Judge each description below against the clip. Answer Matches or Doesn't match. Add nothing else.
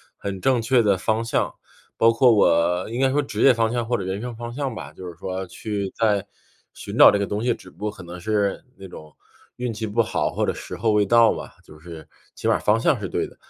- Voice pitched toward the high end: Doesn't match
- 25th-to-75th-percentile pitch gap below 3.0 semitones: Doesn't match